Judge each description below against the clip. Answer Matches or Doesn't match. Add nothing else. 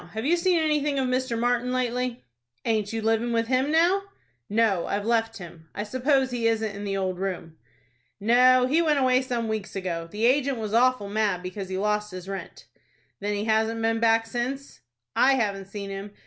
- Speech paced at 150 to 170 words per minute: Doesn't match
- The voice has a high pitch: Matches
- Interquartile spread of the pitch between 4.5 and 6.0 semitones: Doesn't match